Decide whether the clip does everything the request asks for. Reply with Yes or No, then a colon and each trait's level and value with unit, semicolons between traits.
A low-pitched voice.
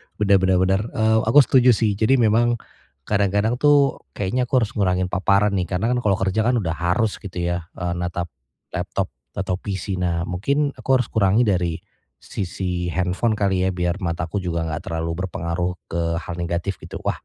Yes: very low, 95 Hz